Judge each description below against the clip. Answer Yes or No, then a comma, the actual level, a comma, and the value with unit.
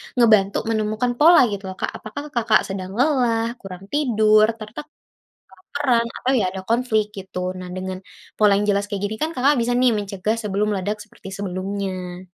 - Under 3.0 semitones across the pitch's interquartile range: No, average, 3.3 semitones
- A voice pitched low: No, high, 215 Hz